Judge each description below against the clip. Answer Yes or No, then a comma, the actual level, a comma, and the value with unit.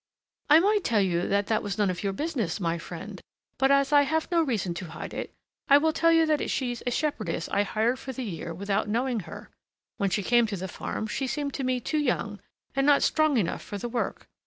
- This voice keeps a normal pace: No, fast, 235 wpm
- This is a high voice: Yes, high, 235 Hz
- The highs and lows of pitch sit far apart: Yes, wide, 6.3 semitones